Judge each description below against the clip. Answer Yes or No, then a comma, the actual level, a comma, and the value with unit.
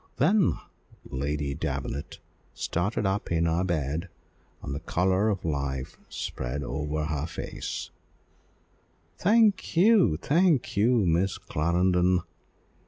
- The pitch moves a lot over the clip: Yes, wide, 5.8 semitones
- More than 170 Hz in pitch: No, very low, 85 Hz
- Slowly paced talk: Yes, slow, 105 wpm